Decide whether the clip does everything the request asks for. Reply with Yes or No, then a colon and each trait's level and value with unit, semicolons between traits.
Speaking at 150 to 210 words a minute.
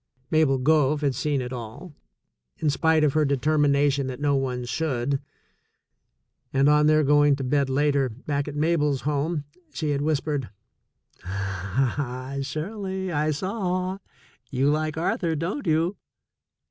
No: average, 140 wpm